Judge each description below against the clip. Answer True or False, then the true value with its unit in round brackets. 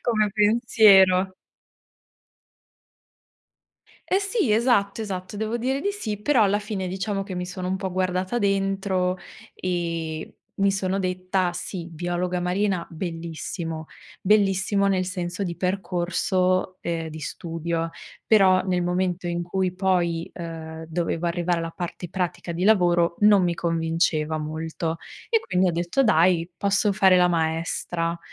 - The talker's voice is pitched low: False (185 Hz)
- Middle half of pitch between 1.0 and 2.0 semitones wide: False (2.5 semitones)